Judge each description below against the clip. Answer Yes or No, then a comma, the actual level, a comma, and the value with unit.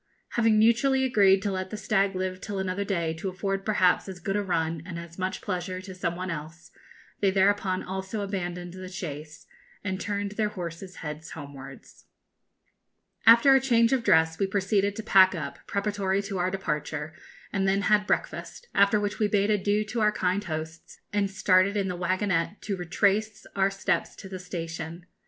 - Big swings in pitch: No, narrow, 2.5 semitones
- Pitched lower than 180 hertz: No, high, 190 Hz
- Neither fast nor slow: Yes, average, 185 wpm